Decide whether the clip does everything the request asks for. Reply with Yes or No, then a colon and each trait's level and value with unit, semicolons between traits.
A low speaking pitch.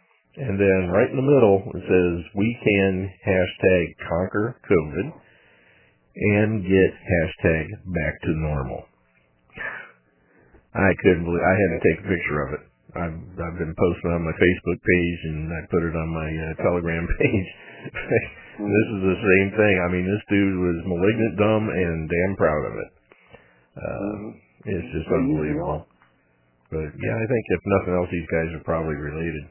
Yes: very low, 90 Hz